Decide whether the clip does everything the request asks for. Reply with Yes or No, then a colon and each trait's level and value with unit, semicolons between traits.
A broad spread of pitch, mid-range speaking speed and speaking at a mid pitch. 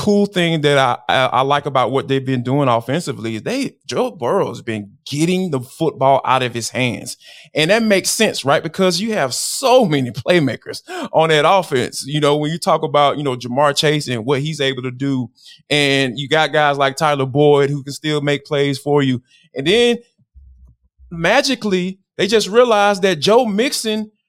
Yes: wide, 5.7 semitones; average, 195 wpm; medium, 145 Hz